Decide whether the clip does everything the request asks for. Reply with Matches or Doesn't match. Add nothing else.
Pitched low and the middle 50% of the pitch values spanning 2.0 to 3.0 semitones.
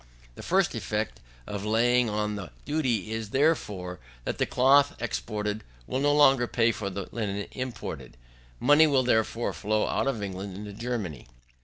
Doesn't match